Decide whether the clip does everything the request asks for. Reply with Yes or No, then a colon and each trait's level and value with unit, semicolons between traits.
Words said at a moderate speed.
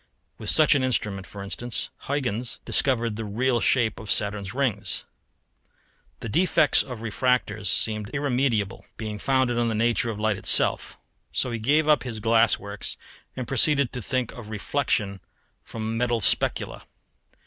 Yes: average, 150 wpm